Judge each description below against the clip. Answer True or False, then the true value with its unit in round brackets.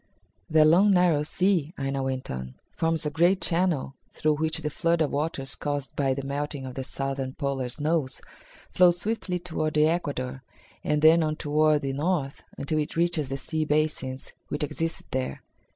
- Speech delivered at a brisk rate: False (175 wpm)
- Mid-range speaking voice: True (150 Hz)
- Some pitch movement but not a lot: True (3.1 semitones)